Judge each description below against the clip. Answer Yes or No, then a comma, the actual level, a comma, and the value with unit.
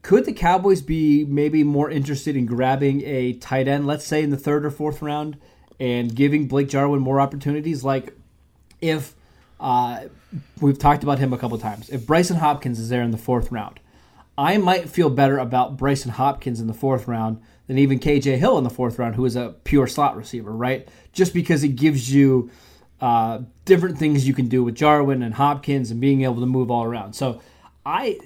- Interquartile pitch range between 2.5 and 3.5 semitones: Yes, average, 3.2 semitones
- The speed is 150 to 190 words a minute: No, fast, 205 wpm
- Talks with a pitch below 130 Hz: No, low, 135 Hz